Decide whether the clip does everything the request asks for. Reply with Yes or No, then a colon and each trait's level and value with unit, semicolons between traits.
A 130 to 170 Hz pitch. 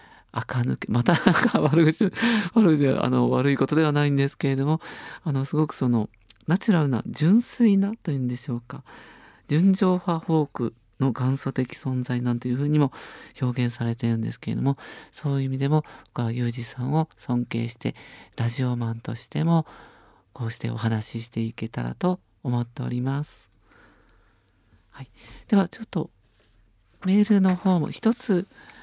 Yes: low, 135 Hz